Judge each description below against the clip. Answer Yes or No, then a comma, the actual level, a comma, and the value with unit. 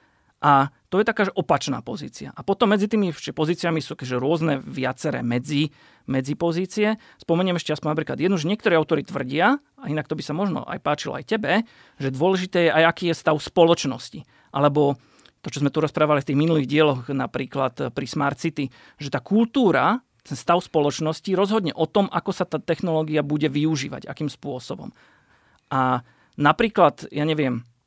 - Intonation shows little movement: No, average, 4.2 semitones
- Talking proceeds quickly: Yes, fast, 170 wpm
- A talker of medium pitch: Yes, medium, 155 Hz